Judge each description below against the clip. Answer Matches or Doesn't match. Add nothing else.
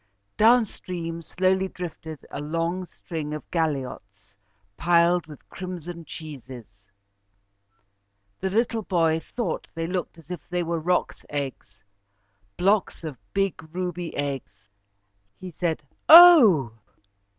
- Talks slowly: Matches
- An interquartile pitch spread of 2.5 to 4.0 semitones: Matches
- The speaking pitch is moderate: Matches